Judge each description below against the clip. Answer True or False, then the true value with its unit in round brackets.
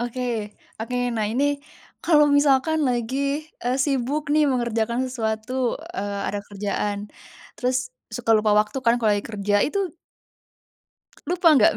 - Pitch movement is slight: False (4.2 semitones)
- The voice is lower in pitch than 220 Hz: False (245 Hz)